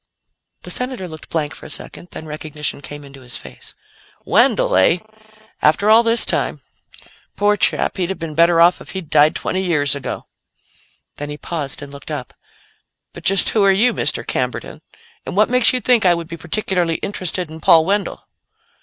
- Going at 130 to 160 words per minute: No, average, 185 wpm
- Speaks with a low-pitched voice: No, medium, 170 Hz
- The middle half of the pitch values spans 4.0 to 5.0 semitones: Yes, average, 4.7 semitones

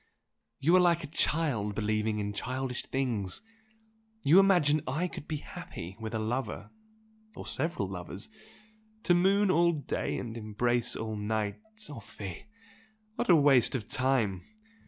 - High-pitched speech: No, low, 125 Hz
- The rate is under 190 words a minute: Yes, average, 145 wpm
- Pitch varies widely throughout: Yes, wide, 6.7 semitones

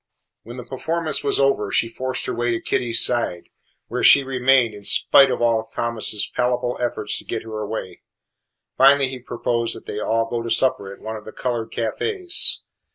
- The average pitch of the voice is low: Yes, low, 120 Hz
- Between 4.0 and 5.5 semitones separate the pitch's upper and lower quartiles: No, average, 2.7 semitones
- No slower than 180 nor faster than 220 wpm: Yes, average, 190 wpm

